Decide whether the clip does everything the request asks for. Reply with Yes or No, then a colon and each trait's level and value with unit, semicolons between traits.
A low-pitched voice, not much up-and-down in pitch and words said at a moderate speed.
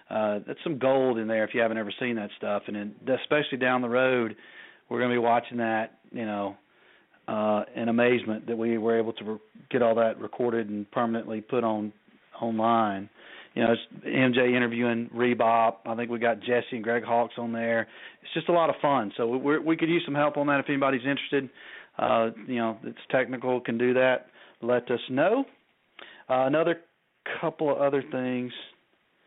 Yes: low, 120 Hz; narrow, 2.3 semitones; average, 195 wpm